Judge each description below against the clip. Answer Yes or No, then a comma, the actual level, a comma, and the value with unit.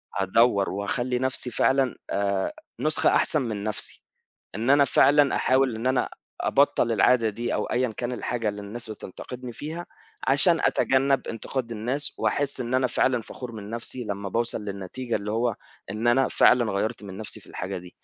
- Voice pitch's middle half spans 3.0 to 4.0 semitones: Yes, average, 3.6 semitones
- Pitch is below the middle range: Yes, low, 120 Hz